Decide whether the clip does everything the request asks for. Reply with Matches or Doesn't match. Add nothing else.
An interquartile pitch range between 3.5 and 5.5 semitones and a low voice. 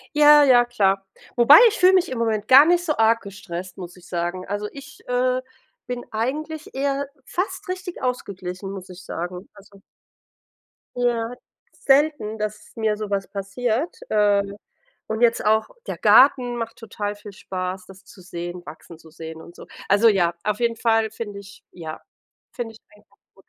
Doesn't match